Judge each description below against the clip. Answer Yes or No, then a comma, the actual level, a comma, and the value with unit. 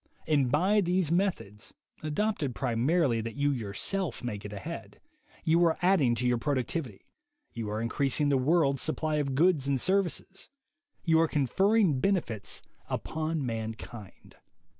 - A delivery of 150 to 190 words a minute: No, average, 140 wpm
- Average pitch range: No, wide, 6.2 semitones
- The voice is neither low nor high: Yes, medium, 145 Hz